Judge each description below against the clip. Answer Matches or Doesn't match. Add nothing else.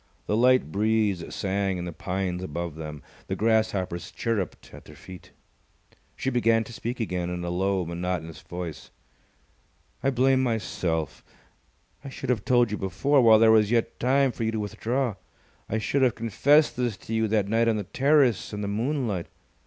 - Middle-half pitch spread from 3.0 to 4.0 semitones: Doesn't match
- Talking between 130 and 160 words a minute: Doesn't match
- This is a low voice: Matches